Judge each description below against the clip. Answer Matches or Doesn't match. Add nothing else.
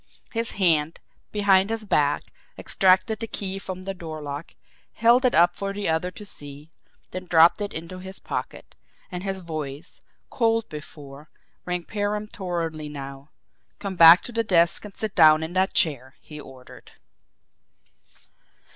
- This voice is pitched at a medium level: Matches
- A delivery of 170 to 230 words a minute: Doesn't match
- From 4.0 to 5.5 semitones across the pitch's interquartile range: Matches